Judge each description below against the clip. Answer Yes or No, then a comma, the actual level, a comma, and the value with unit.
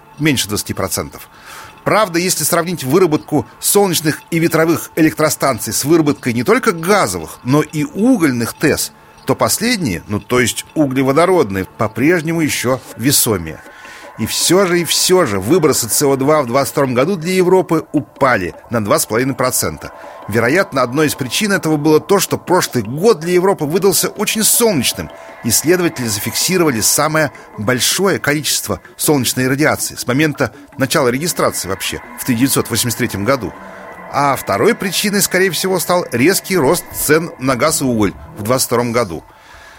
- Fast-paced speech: No, average, 135 wpm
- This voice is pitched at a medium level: Yes, medium, 145 Hz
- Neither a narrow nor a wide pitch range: No, wide, 6.3 semitones